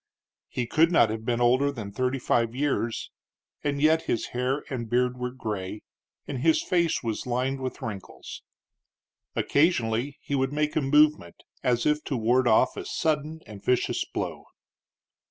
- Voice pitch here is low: Yes, low, 130 Hz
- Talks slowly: No, average, 160 wpm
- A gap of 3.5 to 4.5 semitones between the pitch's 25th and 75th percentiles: Yes, average, 3.8 semitones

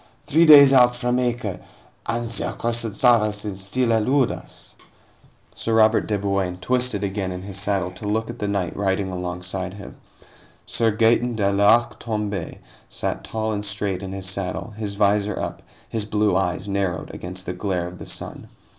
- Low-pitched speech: Yes, low, 105 Hz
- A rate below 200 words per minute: Yes, average, 170 wpm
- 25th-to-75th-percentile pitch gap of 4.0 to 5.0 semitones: No, average, 3.0 semitones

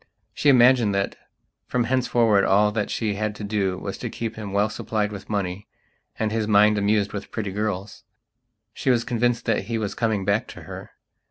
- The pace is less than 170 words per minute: No, average, 190 wpm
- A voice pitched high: No, low, 105 Hz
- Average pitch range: No, narrow, 2.1 semitones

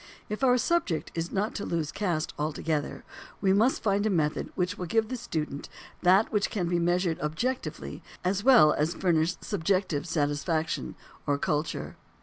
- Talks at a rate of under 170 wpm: Yes, average, 160 wpm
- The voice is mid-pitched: Yes, medium, 180 Hz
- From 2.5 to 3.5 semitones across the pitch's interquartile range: No, average, 4.6 semitones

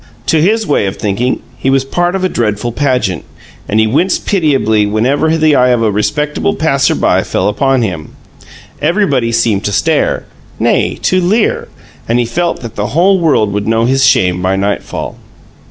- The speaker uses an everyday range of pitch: No, wide, 6.9 semitones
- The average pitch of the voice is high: No, low, 125 Hz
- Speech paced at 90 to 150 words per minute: No, average, 180 wpm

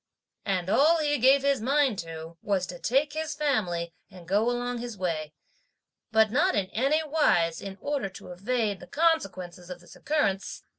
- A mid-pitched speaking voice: No, high, 220 Hz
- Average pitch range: No, wide, 7.7 semitones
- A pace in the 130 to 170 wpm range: No, average, 180 wpm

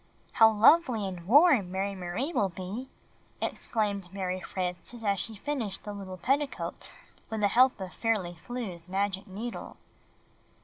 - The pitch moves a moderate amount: Yes, average, 4.2 semitones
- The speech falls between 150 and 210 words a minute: No, average, 140 wpm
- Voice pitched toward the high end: Yes, high, 200 Hz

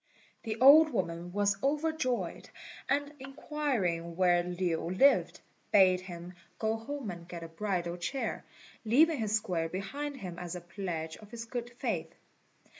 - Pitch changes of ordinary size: No, wide, 7.1 semitones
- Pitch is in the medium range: No, high, 200 Hz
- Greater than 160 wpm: No, average, 145 wpm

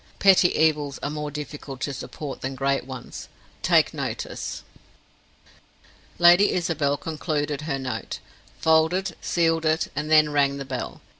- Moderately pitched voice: Yes, medium, 150 Hz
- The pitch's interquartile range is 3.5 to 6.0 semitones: No, narrow, 2.4 semitones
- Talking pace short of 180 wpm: Yes, slow, 135 wpm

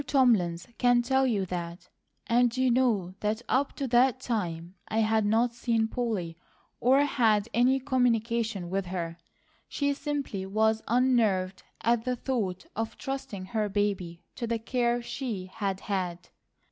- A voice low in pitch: No, high, 225 Hz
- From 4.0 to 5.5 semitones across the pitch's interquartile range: Yes, average, 4.4 semitones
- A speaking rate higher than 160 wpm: No, average, 145 wpm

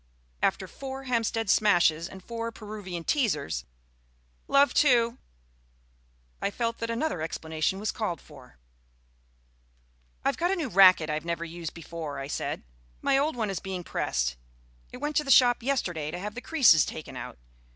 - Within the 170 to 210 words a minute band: No, average, 160 wpm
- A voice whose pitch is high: Yes, high, 200 Hz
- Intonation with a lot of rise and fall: Yes, wide, 6.9 semitones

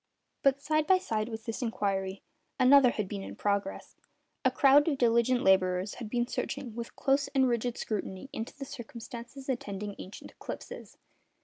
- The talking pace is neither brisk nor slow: Yes, average, 165 wpm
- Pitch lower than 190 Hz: No, high, 235 Hz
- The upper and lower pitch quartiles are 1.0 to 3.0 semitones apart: No, average, 4.5 semitones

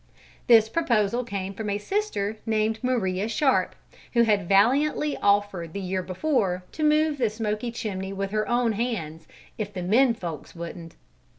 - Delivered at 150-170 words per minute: Yes, average, 160 wpm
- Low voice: No, high, 215 Hz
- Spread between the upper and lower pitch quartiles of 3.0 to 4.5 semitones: Yes, average, 4.0 semitones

